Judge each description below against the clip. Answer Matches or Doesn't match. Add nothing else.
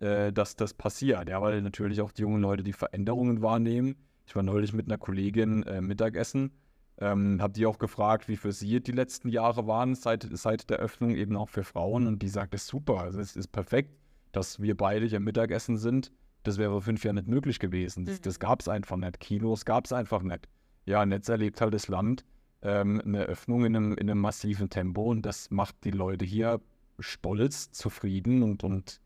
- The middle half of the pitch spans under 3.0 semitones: Matches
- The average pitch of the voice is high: Doesn't match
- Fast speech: Matches